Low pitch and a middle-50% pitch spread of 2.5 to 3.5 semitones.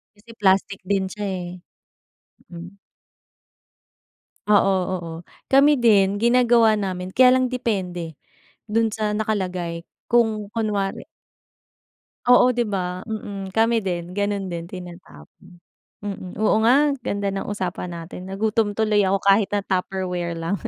No: high, 200 Hz; average, 3.2 semitones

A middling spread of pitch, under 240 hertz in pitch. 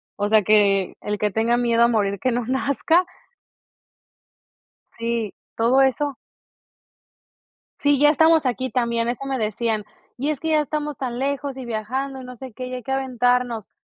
No: average, 3.0 semitones; very high, 250 Hz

